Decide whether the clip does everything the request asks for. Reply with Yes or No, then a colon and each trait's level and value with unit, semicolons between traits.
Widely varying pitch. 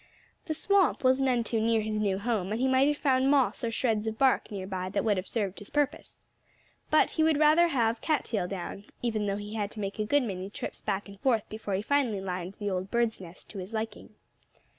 No: average, 4.6 semitones